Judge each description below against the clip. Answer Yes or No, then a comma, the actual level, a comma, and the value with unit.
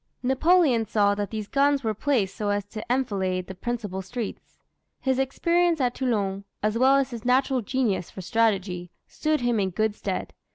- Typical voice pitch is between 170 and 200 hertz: No, high, 230 Hz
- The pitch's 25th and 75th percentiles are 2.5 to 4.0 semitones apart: No, average, 4.7 semitones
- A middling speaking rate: Yes, average, 175 wpm